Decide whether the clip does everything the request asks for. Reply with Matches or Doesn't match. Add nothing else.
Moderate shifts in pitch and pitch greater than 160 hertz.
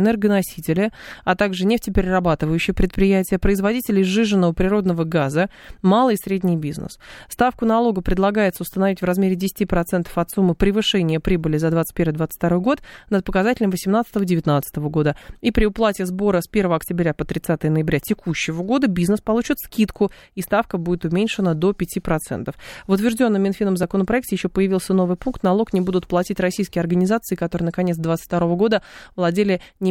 Matches